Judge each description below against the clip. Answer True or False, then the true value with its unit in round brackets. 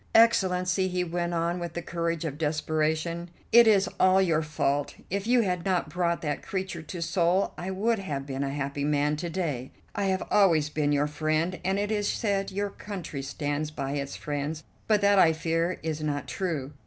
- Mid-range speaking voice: True (170 Hz)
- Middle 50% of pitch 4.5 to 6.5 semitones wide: False (4.0 semitones)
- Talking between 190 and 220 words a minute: True (195 wpm)